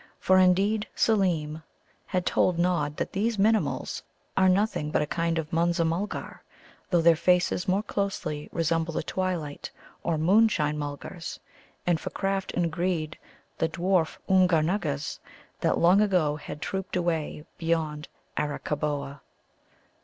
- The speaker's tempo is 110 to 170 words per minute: Yes, slow, 135 wpm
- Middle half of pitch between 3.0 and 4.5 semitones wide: Yes, average, 3.4 semitones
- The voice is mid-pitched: Yes, medium, 170 Hz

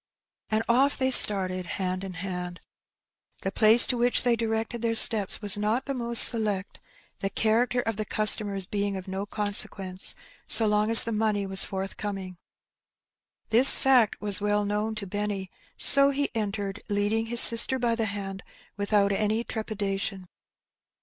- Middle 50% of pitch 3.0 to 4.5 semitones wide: No, narrow, 2.5 semitones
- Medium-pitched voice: No, high, 210 Hz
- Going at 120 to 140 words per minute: No, average, 160 wpm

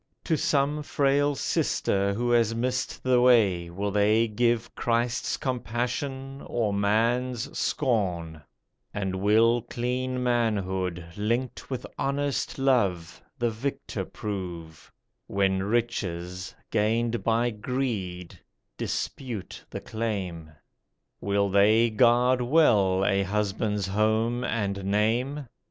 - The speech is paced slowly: Yes, slow, 105 wpm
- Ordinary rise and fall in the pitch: Yes, average, 3.9 semitones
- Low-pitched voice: Yes, low, 115 Hz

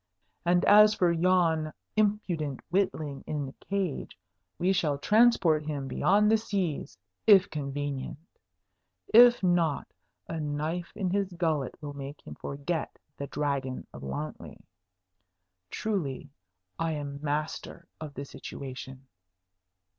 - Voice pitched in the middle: Yes, medium, 155 Hz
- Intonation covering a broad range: No, average, 4.8 semitones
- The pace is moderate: No, slow, 120 wpm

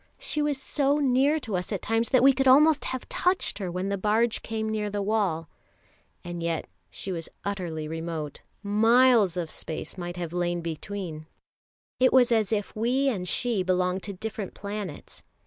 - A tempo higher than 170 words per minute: Yes, average, 180 wpm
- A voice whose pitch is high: Yes, high, 205 Hz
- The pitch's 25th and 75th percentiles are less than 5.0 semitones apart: No, wide, 5.6 semitones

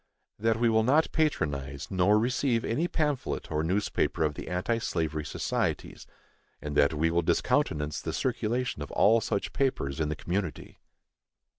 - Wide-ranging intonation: Yes, wide, 7.4 semitones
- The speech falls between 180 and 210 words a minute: No, average, 155 wpm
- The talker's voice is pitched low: Yes, low, 100 Hz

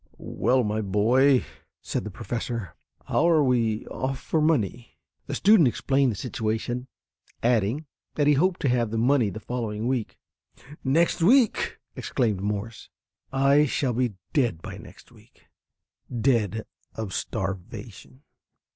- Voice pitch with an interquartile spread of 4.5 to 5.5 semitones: No, average, 4.0 semitones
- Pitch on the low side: Yes, low, 120 Hz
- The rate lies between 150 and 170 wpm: No, slow, 135 wpm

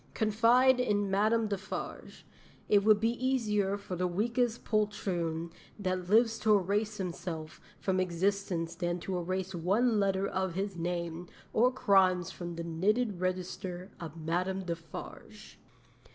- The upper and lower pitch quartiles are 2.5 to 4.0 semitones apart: Yes, average, 3.3 semitones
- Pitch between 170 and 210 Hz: Yes, high, 190 Hz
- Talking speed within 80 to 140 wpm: Yes, slow, 135 wpm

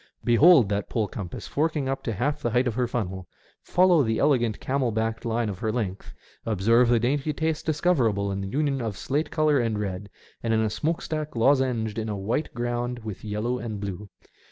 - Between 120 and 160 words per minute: No, fast, 205 wpm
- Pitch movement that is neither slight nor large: Yes, average, 4.7 semitones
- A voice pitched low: Yes, low, 120 Hz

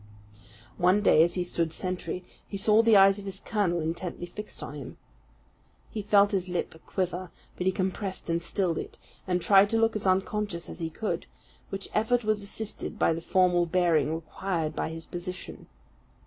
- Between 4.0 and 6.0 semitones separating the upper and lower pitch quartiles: No, average, 2.9 semitones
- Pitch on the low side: No, medium, 185 Hz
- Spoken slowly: No, average, 180 wpm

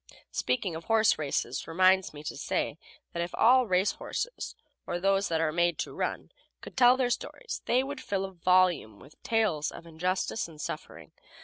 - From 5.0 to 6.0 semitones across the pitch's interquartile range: Yes, wide, 5.4 semitones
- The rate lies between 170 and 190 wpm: Yes, average, 180 wpm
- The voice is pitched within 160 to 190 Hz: Yes, medium, 185 Hz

